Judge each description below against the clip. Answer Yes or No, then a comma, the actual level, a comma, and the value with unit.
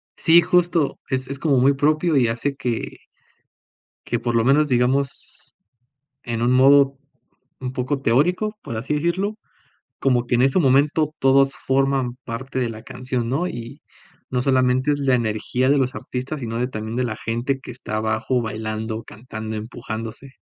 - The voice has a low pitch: Yes, low, 130 Hz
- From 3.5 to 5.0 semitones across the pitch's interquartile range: No, average, 3.0 semitones